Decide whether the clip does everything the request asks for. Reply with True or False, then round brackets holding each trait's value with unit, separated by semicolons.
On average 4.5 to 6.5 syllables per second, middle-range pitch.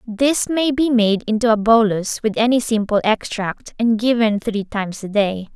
False (4.6 syllables/s; 220 Hz)